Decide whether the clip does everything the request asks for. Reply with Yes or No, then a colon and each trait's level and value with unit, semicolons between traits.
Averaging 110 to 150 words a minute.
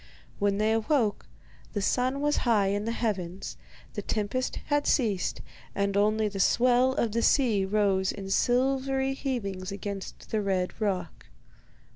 Yes: average, 145 wpm